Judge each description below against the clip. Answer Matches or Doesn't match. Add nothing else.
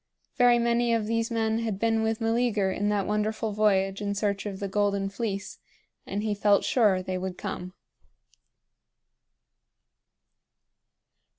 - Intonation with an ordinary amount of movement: Doesn't match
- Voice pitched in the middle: Doesn't match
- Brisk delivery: Doesn't match